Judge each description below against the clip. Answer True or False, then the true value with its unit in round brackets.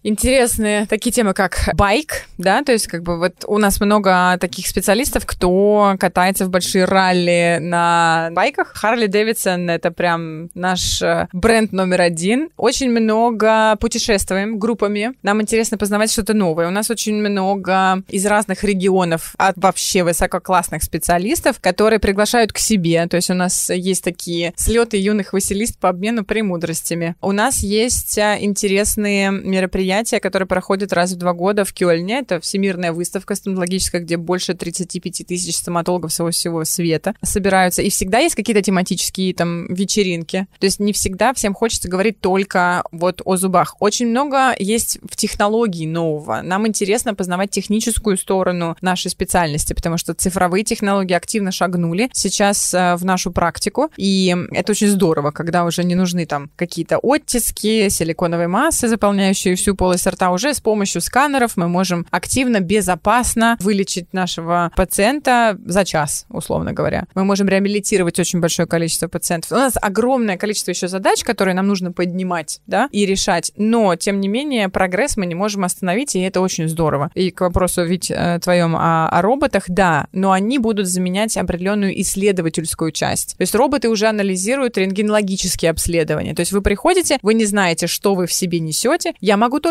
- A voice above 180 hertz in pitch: True (190 Hz)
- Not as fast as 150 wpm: False (160 wpm)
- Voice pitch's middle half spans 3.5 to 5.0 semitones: False (3.1 semitones)